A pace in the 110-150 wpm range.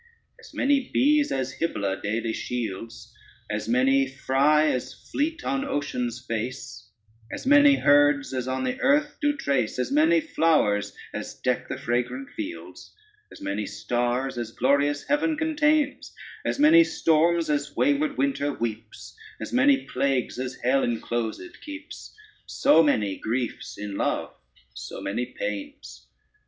Yes: average, 140 wpm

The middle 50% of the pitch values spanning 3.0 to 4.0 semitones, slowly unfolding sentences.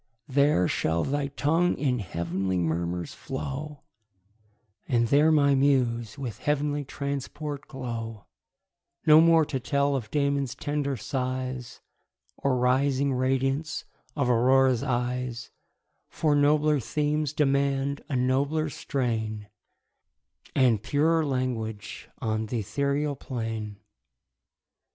Yes: average, 3.3 semitones; slow, 105 wpm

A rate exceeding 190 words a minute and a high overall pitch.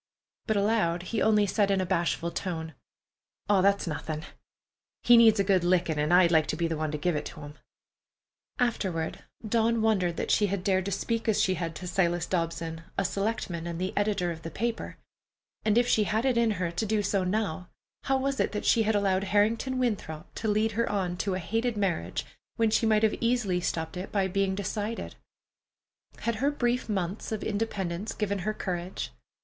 Yes: average, 200 wpm; high, 195 Hz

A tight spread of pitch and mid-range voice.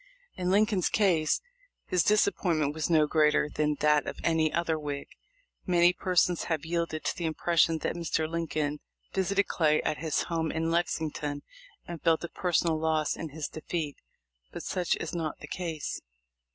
Yes: narrow, 2.0 semitones; medium, 160 Hz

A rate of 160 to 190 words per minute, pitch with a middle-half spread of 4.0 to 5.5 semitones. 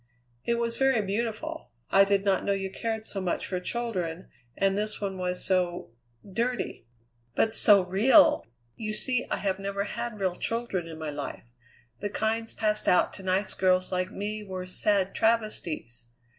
No: average, 170 wpm; average, 3.2 semitones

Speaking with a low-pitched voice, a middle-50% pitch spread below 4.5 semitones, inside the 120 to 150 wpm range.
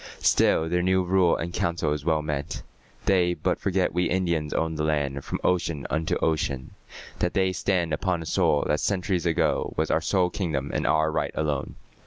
No: very low, 80 Hz; average, 2.8 semitones; average, 190 wpm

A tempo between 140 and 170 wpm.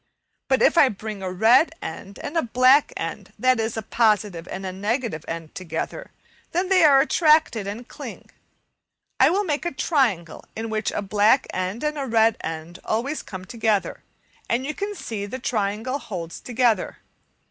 No: average, 180 wpm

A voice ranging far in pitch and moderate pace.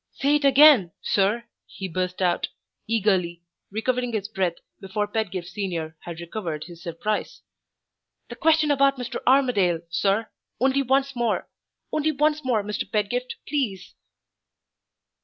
No: wide, 6.3 semitones; slow, 130 wpm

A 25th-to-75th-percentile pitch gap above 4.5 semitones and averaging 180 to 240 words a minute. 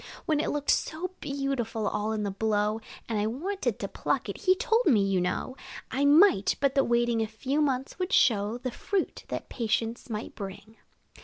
Yes: average, 5.1 semitones; average, 190 wpm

